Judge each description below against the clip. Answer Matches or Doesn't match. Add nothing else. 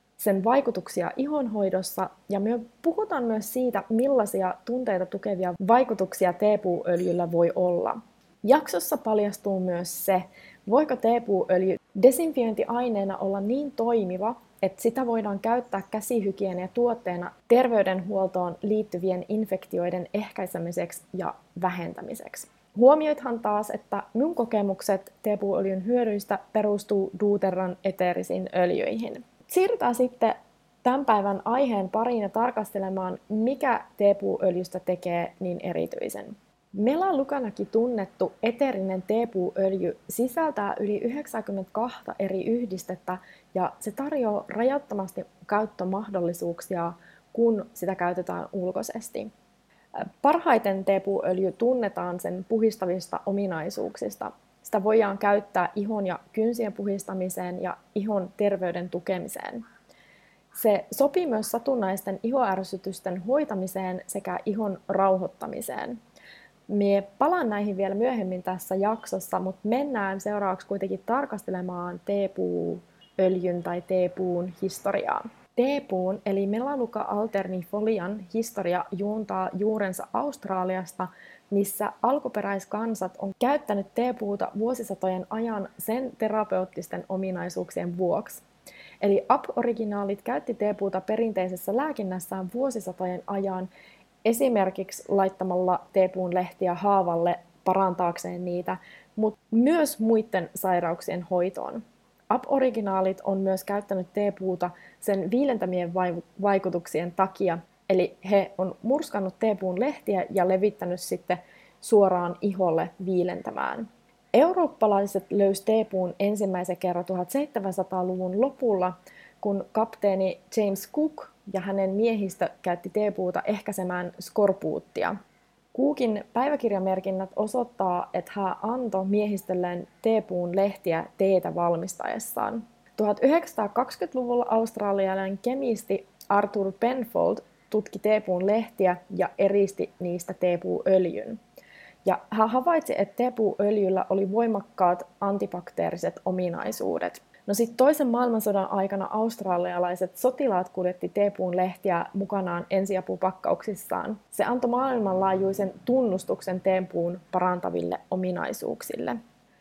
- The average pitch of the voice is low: Doesn't match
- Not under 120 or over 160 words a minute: Doesn't match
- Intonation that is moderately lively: Matches